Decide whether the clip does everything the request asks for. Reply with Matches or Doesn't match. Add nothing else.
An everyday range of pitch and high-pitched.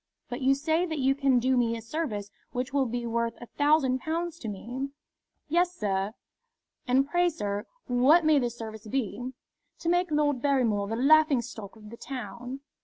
Matches